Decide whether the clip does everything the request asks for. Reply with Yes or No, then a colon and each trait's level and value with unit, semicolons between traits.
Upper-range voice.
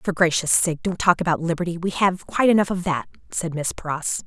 No: medium, 170 Hz